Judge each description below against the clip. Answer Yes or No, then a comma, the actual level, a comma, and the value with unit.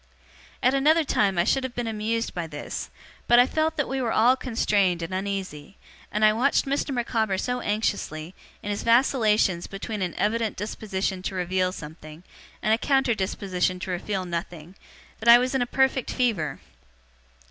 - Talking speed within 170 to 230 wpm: Yes, average, 175 wpm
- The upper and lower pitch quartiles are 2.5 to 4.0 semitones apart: No, average, 5.0 semitones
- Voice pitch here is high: Yes, high, 210 Hz